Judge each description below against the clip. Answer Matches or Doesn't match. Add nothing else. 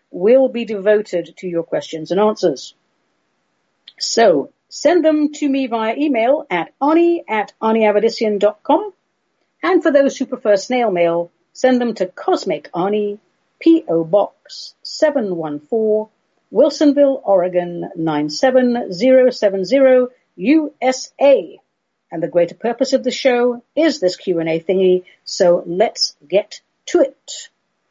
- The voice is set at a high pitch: Matches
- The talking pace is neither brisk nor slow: Doesn't match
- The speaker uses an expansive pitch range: Matches